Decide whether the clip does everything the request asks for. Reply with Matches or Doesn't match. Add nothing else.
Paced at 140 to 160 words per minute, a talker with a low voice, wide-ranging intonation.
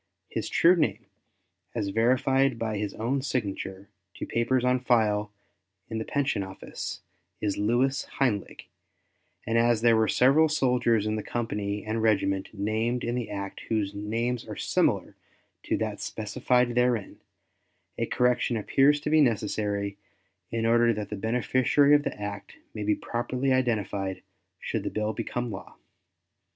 Doesn't match